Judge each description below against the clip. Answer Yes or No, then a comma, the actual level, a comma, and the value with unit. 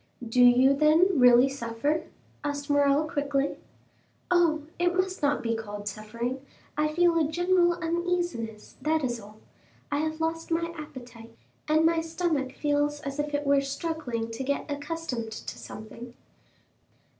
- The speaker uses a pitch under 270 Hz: No, very high, 290 Hz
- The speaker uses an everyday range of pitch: Yes, average, 4.9 semitones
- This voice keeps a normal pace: Yes, average, 145 wpm